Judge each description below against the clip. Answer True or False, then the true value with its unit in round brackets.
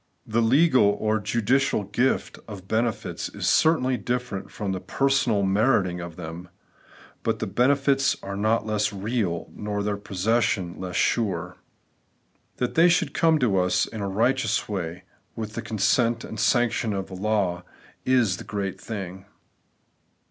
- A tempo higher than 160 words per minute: False (145 wpm)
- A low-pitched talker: True (110 Hz)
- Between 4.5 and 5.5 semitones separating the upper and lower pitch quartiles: False (4.0 semitones)